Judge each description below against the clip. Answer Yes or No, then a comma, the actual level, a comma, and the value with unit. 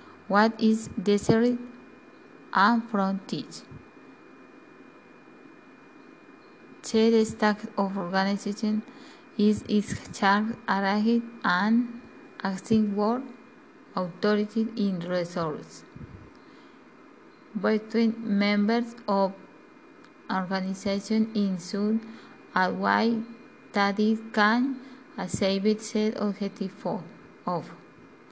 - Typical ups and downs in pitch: Yes, average, 3.0 semitones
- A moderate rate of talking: No, slow, 70 wpm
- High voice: Yes, high, 215 Hz